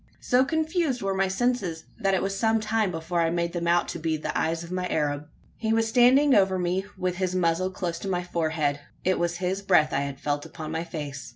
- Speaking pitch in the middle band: Yes, medium, 180 Hz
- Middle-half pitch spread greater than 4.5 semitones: No, average, 3.3 semitones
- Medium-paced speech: No, fast, 230 wpm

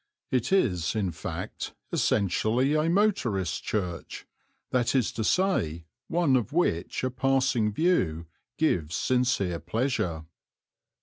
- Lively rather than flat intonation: Yes, wide, 7.4 semitones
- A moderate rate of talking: No, slow, 115 wpm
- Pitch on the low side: Yes, low, 120 Hz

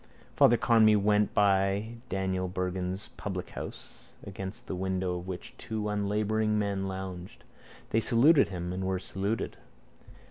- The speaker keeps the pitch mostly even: Yes, narrow, 2.3 semitones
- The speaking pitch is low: Yes, very low, 95 Hz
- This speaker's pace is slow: Yes, slow, 130 wpm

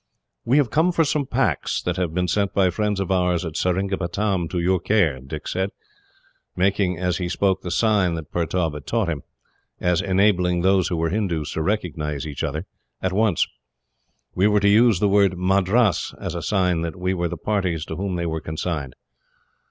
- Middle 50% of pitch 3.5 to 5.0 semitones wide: No, average, 3.1 semitones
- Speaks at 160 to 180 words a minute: No, average, 195 wpm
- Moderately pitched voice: No, very low, 90 Hz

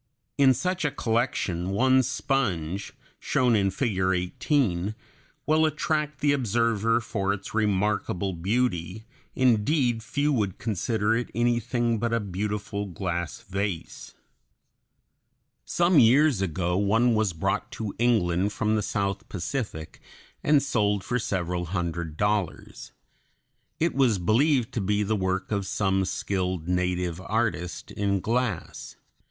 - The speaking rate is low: Yes, slow, 125 wpm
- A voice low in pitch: Yes, low, 105 Hz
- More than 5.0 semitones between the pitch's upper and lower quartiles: No, average, 4.4 semitones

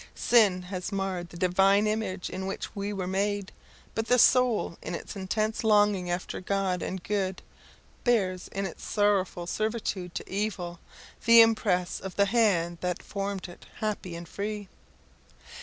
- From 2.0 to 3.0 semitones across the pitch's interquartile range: Yes, narrow, 2.6 semitones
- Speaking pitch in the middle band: No, high, 195 Hz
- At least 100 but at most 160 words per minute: Yes, average, 155 wpm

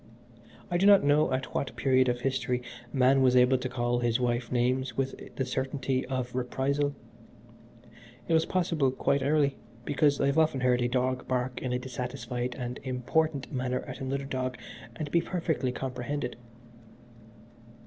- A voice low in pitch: Yes, low, 130 Hz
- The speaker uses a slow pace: No, average, 160 wpm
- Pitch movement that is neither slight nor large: No, narrow, 2.0 semitones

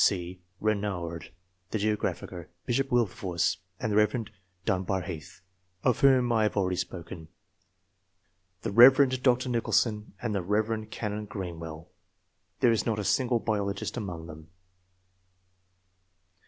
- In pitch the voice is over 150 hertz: No, low, 105 Hz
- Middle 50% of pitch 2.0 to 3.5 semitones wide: No, average, 4.3 semitones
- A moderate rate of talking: No, slow, 125 wpm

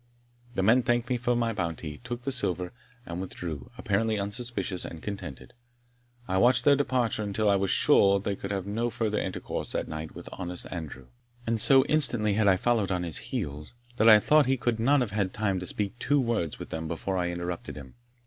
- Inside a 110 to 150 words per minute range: No, fast, 205 wpm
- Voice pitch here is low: Yes, low, 100 Hz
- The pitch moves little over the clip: No, average, 5.1 semitones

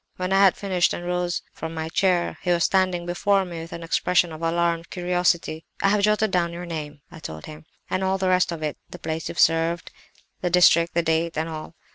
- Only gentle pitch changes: Yes, narrow, 1.9 semitones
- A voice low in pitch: No, medium, 170 Hz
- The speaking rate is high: Yes, fast, 225 wpm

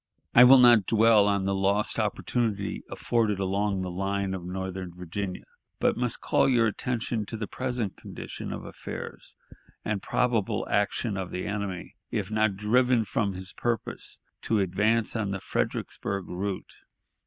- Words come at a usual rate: Yes, average, 155 wpm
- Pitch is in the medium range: No, low, 100 Hz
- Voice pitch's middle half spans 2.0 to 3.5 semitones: Yes, average, 3.0 semitones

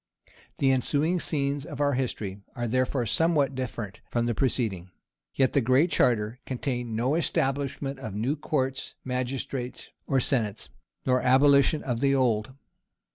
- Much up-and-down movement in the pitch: No, average, 2.7 semitones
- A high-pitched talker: No, low, 130 Hz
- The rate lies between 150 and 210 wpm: No, average, 140 wpm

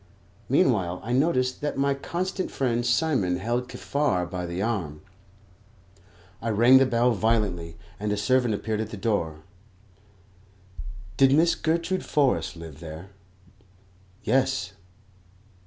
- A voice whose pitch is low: Yes, low, 115 Hz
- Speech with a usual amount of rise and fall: No, wide, 6.1 semitones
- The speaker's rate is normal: No, slow, 125 wpm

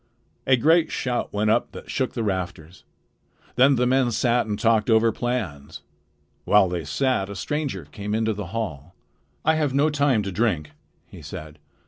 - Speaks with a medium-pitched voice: No, low, 110 Hz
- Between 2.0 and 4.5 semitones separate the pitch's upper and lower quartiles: No, average, 5.1 semitones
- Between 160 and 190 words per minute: Yes, average, 170 wpm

